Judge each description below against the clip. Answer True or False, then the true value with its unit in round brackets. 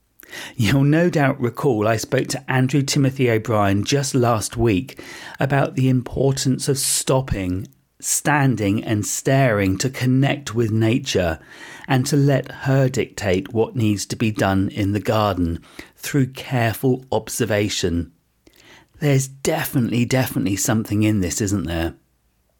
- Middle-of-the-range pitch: False (125 Hz)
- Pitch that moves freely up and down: False (4.6 semitones)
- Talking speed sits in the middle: False (130 wpm)